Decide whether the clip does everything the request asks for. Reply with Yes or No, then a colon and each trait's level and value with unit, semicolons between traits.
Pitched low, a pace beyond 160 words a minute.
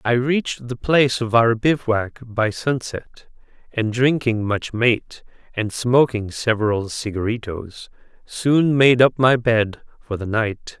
No: low, 120 Hz; average, 140 wpm